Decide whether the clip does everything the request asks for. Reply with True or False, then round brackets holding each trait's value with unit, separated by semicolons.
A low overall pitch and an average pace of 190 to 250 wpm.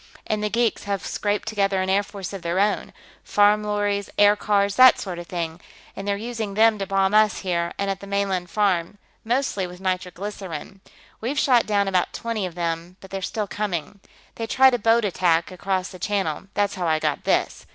False (200 Hz; 205 wpm)